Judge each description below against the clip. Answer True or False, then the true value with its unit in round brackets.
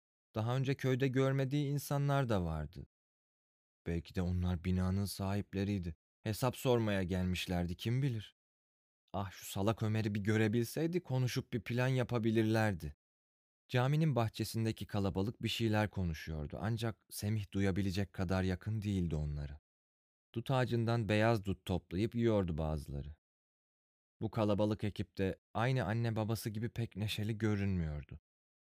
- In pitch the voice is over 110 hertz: False (105 Hz)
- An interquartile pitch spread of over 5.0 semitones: False (4.3 semitones)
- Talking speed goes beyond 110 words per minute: True (120 wpm)